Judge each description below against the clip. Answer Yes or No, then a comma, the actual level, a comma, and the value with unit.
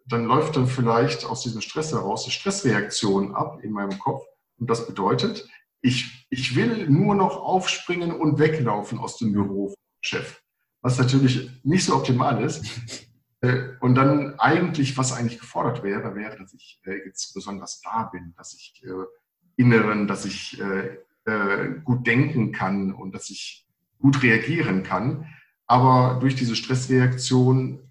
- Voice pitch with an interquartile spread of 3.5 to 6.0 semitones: Yes, average, 4.4 semitones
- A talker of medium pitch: No, low, 125 Hz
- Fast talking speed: No, average, 145 wpm